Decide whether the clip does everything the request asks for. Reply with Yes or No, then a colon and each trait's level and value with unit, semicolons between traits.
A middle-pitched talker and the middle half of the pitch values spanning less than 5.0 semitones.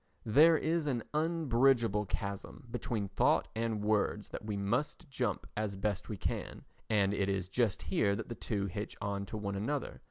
No: low, 105 Hz; average, 3.7 semitones